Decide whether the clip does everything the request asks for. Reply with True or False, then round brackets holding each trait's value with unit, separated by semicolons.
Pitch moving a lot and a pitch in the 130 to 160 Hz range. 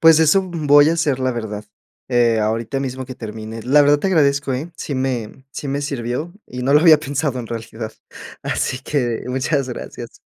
False (3.6 semitones; 135 Hz)